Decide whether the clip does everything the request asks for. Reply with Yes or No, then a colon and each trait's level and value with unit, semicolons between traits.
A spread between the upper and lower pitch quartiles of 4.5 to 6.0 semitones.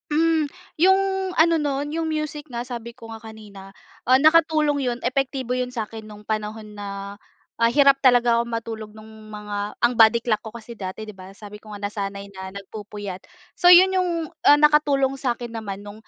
Yes: average, 5.0 semitones